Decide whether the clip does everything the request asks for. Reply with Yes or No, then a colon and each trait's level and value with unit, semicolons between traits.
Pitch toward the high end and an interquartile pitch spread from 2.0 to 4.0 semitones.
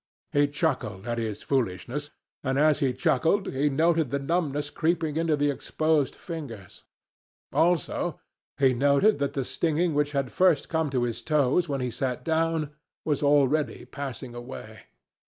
No: medium, 145 Hz; average, 3.4 semitones